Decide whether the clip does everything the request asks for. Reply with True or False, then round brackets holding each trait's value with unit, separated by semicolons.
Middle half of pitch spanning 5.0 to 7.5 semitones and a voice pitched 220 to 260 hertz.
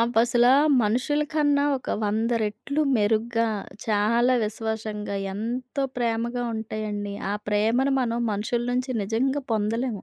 False (2.7 semitones; 230 Hz)